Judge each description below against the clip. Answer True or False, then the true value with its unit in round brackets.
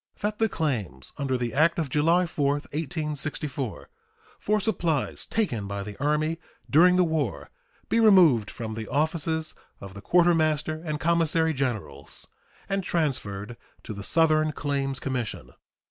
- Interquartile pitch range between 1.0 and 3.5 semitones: False (4.7 semitones)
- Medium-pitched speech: True (150 Hz)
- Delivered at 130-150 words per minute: True (140 wpm)